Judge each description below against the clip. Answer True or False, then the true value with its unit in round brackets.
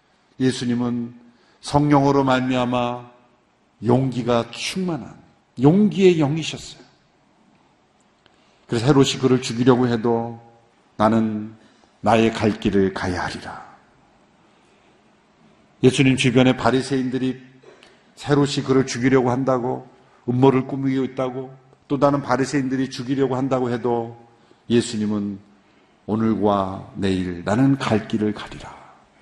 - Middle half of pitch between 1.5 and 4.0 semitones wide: True (2.6 semitones)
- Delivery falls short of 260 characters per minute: True (245 characters per minute)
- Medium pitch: False (125 Hz)